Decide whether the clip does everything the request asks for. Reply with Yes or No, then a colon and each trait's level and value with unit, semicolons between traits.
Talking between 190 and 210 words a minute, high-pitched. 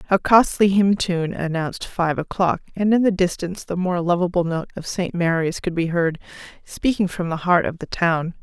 No: average, 200 wpm; medium, 175 Hz